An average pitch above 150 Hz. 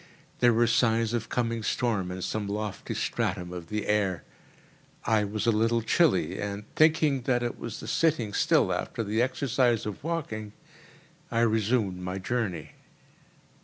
No: low, 110 Hz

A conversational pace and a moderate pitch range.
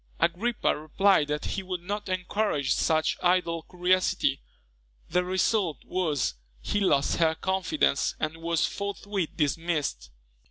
No: slow, 120 wpm; average, 3.4 semitones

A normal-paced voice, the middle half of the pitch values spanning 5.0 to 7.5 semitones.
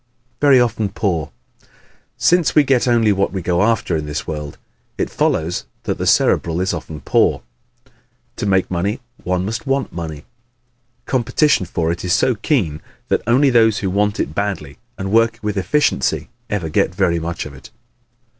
Yes: average, 175 wpm; average, 5.3 semitones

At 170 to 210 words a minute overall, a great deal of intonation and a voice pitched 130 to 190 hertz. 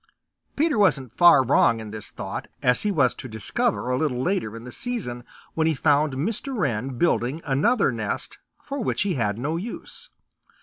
Yes: average, 180 wpm; wide, 8.5 semitones; medium, 140 Hz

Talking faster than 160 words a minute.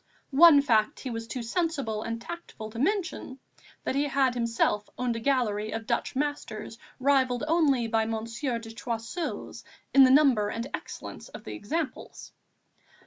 No: average, 155 wpm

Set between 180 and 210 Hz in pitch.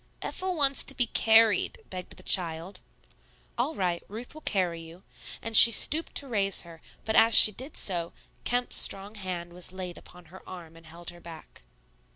Yes: high, 190 Hz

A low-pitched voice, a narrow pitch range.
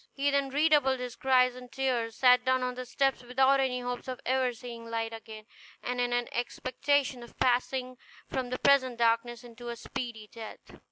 No: very high, 250 Hz; narrow, 1.7 semitones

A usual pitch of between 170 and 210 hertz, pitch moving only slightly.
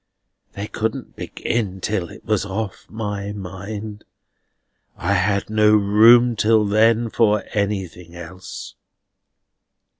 No: low, 105 Hz; narrow, 2.1 semitones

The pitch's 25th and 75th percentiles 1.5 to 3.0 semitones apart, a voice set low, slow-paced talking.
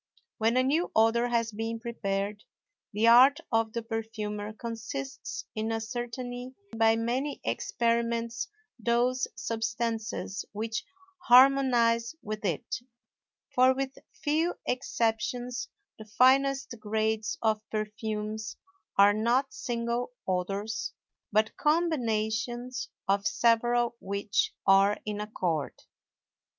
No: narrow, 2.4 semitones; high, 230 Hz; slow, 100 wpm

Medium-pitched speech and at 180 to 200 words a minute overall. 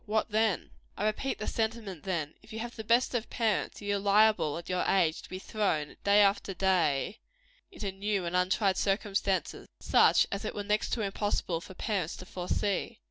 No: high, 200 Hz; average, 190 wpm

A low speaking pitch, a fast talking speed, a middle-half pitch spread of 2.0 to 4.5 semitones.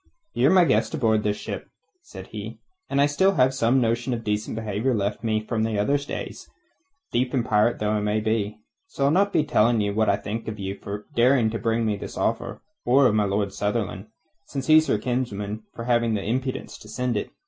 Yes: low, 115 Hz; fast, 215 wpm; average, 3.5 semitones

